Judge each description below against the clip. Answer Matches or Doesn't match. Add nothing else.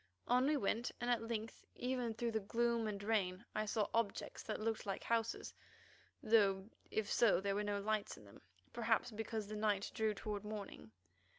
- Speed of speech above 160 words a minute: Matches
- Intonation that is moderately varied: Doesn't match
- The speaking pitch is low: Doesn't match